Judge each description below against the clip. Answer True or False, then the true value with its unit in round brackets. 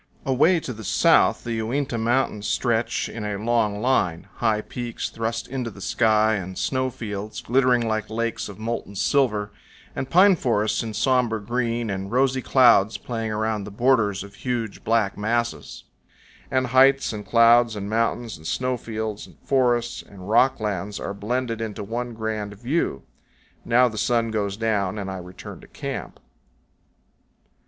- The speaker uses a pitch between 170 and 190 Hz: False (115 Hz)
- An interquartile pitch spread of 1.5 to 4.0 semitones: True (2.7 semitones)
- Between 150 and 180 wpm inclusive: True (160 wpm)